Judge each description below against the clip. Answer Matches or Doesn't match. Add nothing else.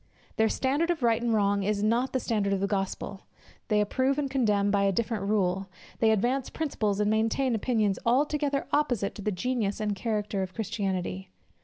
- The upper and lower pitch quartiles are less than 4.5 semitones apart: Matches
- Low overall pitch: Doesn't match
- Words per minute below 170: Doesn't match